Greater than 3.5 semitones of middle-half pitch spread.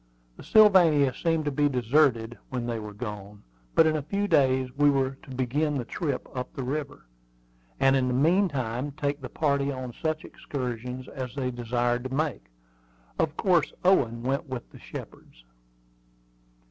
No: average, 3.2 semitones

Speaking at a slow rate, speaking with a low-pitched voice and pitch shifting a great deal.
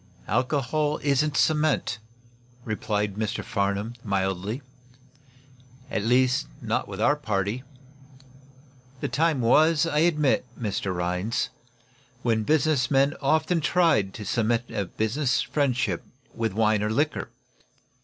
Yes: slow, 115 wpm; low, 120 Hz; wide, 5.8 semitones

